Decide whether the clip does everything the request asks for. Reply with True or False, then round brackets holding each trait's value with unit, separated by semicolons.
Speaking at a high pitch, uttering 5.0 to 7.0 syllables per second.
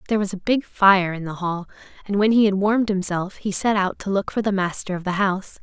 True (195 Hz; 6.0 syllables/s)